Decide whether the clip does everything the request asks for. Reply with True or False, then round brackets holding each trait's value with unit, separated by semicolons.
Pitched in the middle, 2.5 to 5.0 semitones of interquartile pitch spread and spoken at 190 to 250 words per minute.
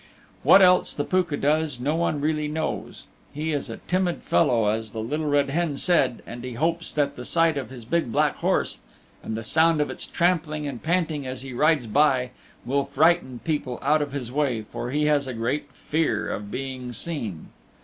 True (145 Hz; 4.1 semitones; 200 wpm)